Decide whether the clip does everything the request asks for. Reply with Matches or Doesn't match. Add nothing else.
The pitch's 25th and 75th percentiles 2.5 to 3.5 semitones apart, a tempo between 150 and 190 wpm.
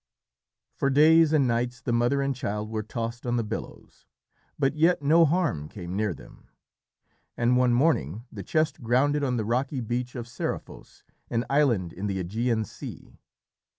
Doesn't match